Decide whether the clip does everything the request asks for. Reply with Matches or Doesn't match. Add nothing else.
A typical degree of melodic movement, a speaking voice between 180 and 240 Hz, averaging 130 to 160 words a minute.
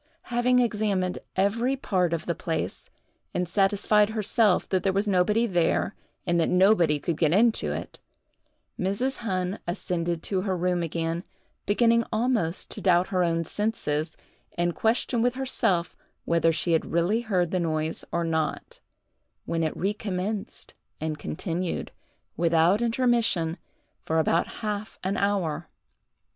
Matches